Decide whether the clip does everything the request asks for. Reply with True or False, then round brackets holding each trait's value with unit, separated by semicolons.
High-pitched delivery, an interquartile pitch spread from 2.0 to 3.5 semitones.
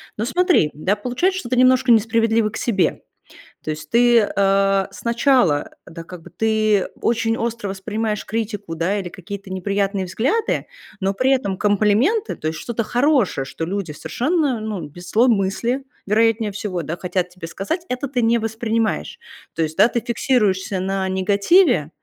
False (210 Hz; 3.9 semitones)